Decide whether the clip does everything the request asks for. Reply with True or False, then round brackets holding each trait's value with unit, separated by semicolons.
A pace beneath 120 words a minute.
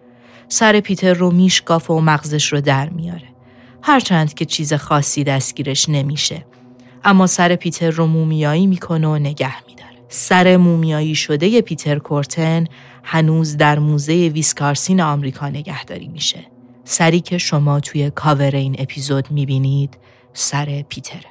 False (130 wpm)